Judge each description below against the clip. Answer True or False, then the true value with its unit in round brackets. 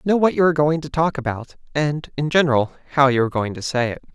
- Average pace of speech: False (260 wpm)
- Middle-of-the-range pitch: True (145 Hz)